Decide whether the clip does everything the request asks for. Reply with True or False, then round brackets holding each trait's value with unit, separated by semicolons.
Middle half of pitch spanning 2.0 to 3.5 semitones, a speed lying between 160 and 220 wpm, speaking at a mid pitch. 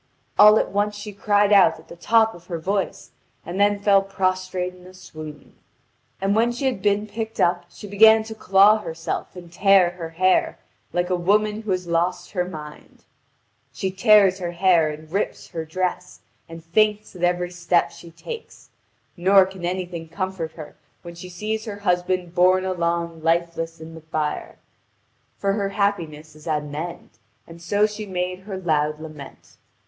True (3.1 semitones; 175 wpm; 180 Hz)